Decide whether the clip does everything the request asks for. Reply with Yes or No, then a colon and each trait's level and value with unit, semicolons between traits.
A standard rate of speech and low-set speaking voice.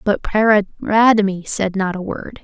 No: average, 150 wpm; high, 200 Hz